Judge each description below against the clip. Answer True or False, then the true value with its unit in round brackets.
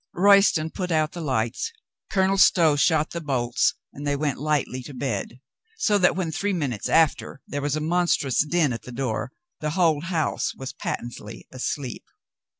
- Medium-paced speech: True (170 wpm)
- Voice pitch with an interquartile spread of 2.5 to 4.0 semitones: False (4.6 semitones)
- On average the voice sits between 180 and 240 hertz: False (150 Hz)